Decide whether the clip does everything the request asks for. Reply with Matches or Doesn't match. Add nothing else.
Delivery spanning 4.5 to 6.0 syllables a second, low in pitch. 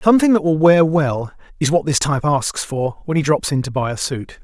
Doesn't match